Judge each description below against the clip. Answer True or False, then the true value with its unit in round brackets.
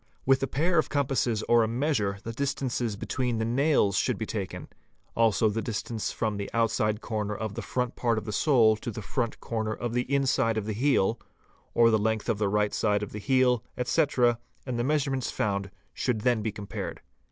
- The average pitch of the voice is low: True (115 Hz)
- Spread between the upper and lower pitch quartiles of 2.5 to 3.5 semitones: True (3.1 semitones)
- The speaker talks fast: True (210 wpm)